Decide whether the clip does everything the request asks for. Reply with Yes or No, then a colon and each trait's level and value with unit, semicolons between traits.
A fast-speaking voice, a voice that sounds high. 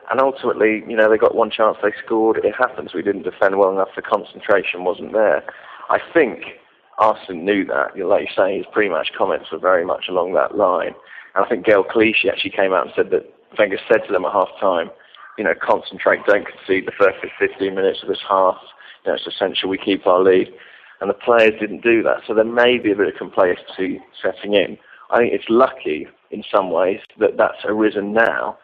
No: fast, 220 wpm; low, 115 Hz